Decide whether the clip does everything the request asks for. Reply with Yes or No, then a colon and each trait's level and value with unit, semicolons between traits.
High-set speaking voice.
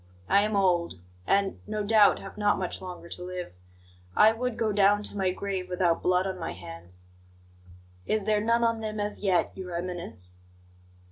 Yes: high, 195 Hz